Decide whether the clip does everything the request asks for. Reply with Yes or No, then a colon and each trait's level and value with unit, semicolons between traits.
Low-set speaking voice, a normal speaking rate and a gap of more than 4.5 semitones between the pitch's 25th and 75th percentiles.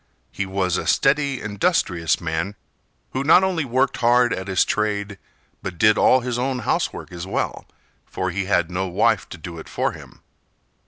Yes: low, 100 Hz; average, 175 wpm; wide, 5.4 semitones